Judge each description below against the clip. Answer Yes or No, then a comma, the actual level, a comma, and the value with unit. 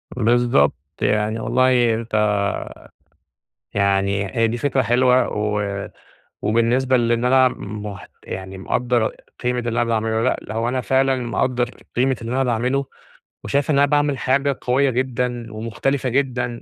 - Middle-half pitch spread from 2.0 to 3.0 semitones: Yes, narrow, 2.6 semitones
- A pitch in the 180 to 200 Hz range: No, low, 120 Hz